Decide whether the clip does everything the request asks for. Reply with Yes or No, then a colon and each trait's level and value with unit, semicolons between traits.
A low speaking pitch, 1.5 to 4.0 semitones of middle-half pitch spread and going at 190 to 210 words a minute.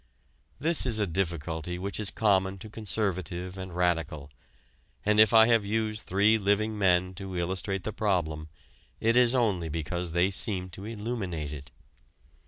No: very low, 95 Hz; average, 3.6 semitones; average, 155 wpm